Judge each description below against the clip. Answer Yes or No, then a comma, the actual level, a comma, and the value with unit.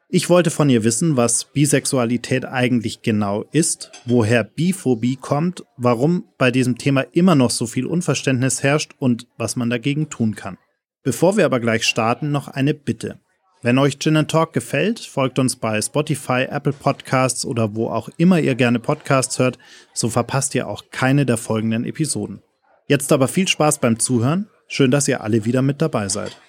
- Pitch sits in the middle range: No, low, 130 Hz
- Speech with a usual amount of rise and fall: Yes, average, 4.0 semitones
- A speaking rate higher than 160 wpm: Yes, average, 175 wpm